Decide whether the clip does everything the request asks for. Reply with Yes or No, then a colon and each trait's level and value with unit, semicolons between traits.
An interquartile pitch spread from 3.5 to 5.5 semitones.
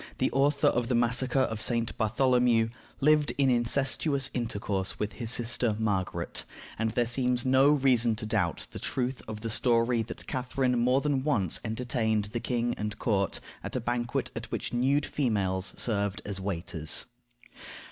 No: average, 3.1 semitones